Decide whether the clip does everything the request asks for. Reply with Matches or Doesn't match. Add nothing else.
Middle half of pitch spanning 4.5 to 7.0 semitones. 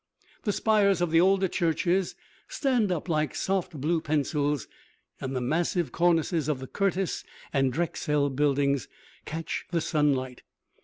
Doesn't match